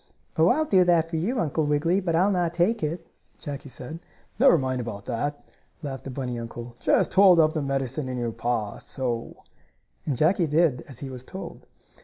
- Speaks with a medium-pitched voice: Yes, medium, 145 Hz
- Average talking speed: Yes, average, 190 wpm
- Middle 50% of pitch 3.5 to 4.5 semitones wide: No, average, 5.3 semitones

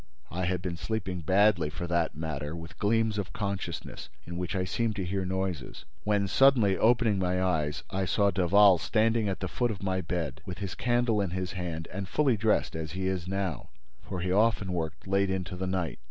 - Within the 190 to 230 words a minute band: Yes, average, 200 wpm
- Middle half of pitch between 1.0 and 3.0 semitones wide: Yes, average, 2.7 semitones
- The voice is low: Yes, very low, 95 Hz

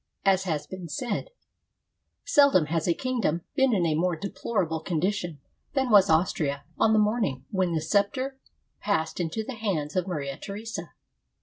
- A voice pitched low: No, medium, 185 Hz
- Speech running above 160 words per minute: Yes, average, 175 wpm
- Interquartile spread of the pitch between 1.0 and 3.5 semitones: No, average, 5.3 semitones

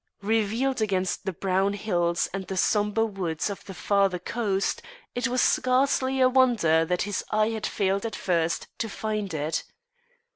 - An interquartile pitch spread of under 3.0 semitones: No, average, 3.4 semitones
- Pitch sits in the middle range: No, high, 200 Hz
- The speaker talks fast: No, average, 160 wpm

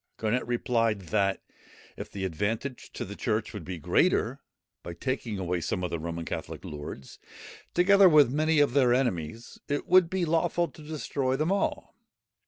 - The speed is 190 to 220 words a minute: No, average, 170 wpm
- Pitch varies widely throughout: Yes, wide, 8.5 semitones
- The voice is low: Yes, low, 120 Hz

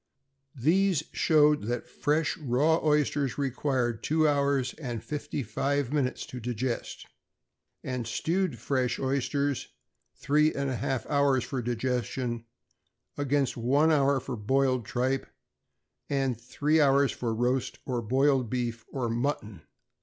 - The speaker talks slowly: Yes, slow, 125 wpm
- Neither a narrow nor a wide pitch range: Yes, average, 3.0 semitones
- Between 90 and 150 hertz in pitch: Yes, low, 135 Hz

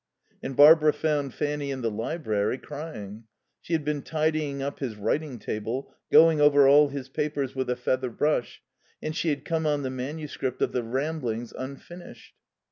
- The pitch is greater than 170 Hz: No, medium, 140 Hz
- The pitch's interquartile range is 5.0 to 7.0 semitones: No, average, 3.2 semitones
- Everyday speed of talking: Yes, average, 170 wpm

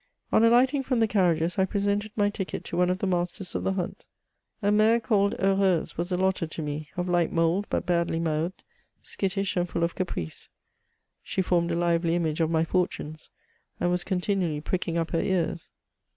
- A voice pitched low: No, medium, 180 Hz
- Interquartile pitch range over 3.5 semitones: No, average, 2.7 semitones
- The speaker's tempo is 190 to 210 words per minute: Yes, average, 195 wpm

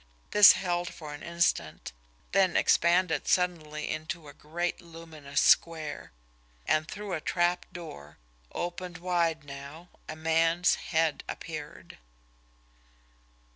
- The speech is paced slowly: Yes, slow, 105 wpm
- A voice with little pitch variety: Yes, narrow, 2.2 semitones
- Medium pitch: Yes, medium, 165 Hz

